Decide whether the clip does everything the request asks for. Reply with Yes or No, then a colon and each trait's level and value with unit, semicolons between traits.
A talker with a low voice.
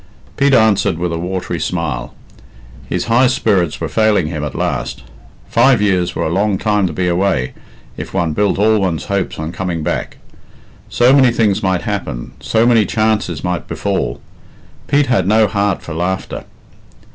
Yes: very low, 95 Hz